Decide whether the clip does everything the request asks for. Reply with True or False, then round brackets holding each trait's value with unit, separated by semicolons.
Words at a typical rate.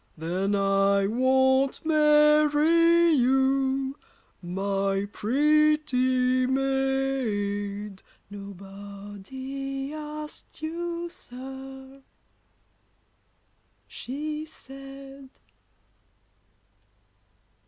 False (50 wpm)